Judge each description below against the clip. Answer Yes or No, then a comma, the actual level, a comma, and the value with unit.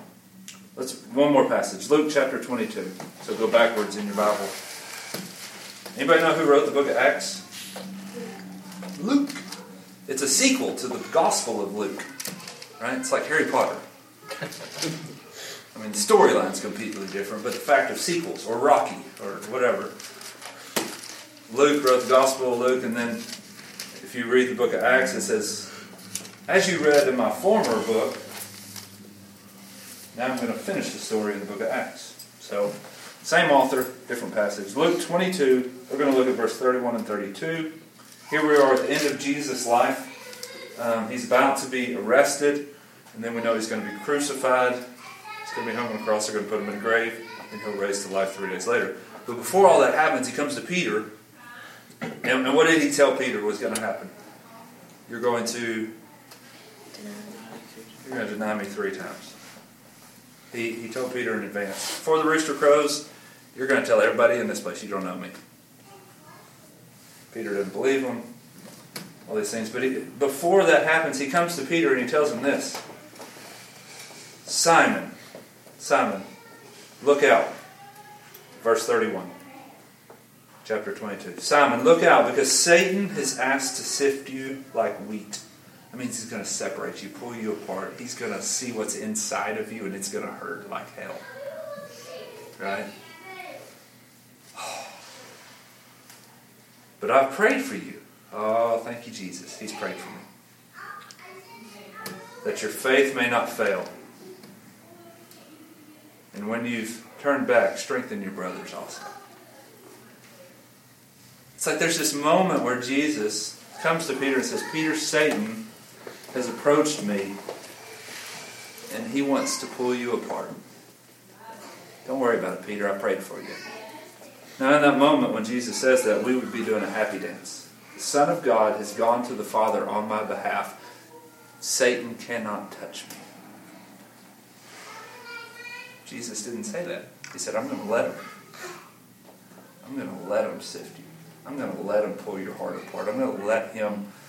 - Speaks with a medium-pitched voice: No, low, 130 Hz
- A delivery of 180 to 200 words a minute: No, average, 165 wpm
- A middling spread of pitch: No, wide, 6.4 semitones